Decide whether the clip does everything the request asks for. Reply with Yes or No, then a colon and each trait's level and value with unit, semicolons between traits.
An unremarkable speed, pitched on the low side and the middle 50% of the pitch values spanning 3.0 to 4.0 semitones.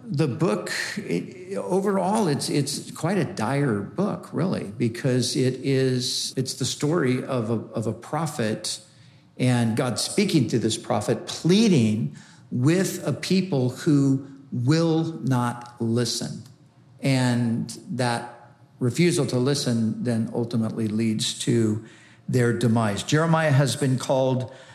No: slow, 125 wpm; low, 125 Hz; average, 3.4 semitones